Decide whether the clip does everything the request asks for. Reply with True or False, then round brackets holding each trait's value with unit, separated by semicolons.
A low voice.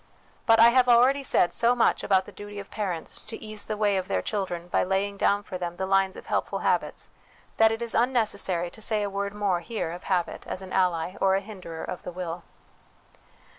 False (200 Hz)